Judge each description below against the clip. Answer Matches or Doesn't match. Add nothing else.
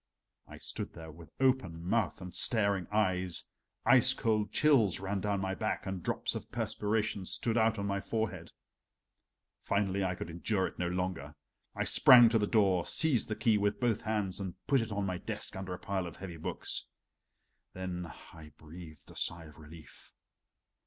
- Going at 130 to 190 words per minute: Matches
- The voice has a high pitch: Doesn't match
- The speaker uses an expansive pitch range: Doesn't match